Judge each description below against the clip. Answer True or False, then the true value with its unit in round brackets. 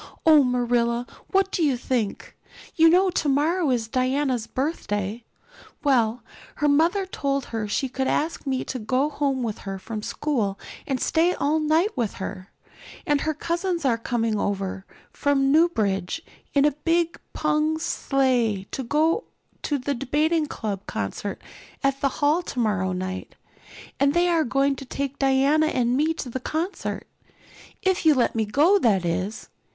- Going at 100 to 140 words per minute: False (155 wpm)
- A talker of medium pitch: False (275 Hz)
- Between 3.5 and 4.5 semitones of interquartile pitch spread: False (5.2 semitones)